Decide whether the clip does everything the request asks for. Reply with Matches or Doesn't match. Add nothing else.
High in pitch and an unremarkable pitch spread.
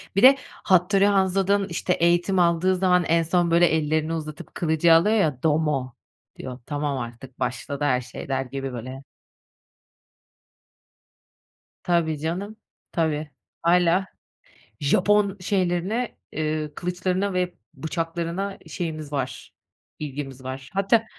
Doesn't match